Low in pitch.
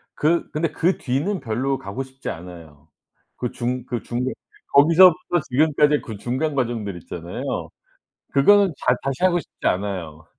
Yes: low, 130 Hz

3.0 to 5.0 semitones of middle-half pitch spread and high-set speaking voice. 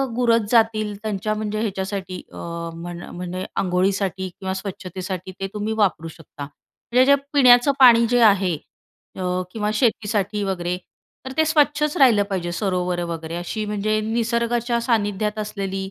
Yes: average, 3.6 semitones; high, 205 Hz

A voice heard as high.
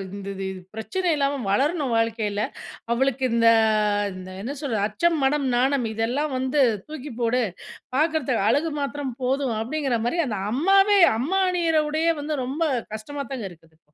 Yes: very high, 270 Hz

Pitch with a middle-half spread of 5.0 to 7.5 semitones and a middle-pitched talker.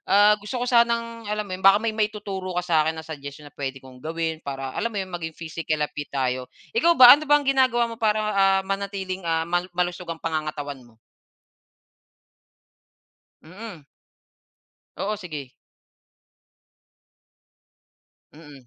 Yes: wide, 5.6 semitones; medium, 180 Hz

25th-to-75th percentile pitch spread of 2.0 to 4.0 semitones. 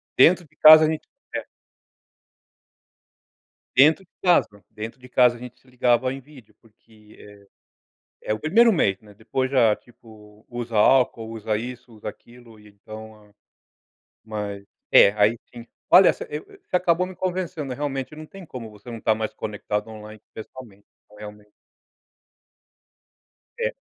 No: average, 4.6 semitones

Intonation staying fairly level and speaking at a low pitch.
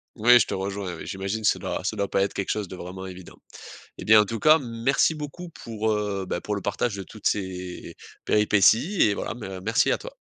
No: average, 3.1 semitones; low, 105 Hz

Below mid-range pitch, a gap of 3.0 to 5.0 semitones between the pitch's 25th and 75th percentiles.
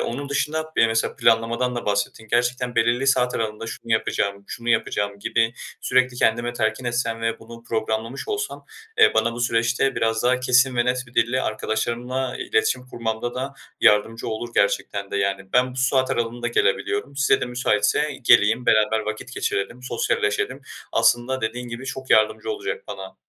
No: low, 120 Hz; narrow, 2.4 semitones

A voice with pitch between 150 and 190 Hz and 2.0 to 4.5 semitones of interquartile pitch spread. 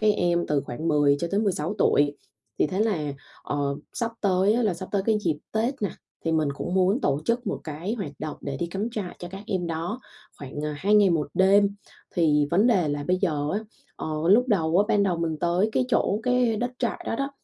No: medium, 185 Hz; average, 5.2 semitones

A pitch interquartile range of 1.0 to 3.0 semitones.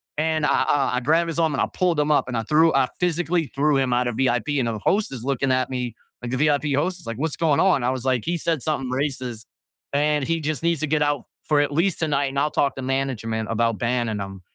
No: average, 3.8 semitones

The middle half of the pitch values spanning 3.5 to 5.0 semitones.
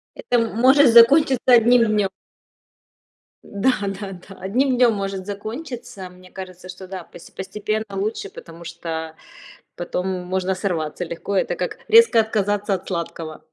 Yes: average, 4.0 semitones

